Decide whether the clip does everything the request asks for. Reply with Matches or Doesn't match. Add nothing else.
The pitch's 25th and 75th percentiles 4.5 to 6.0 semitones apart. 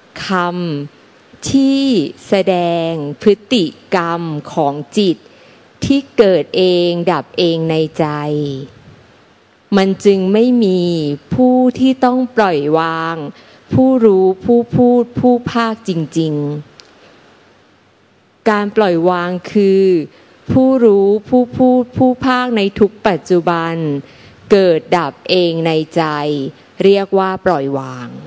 Matches